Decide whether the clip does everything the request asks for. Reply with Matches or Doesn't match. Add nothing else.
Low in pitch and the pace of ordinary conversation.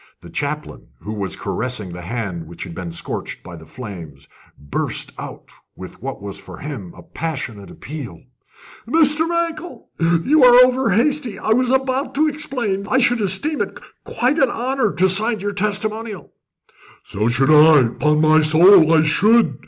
Doesn't match